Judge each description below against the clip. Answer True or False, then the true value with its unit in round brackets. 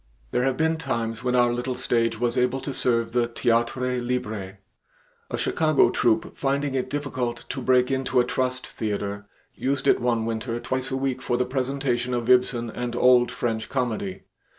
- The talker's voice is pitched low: True (125 Hz)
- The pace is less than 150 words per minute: False (175 wpm)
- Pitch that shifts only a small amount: True (1.9 semitones)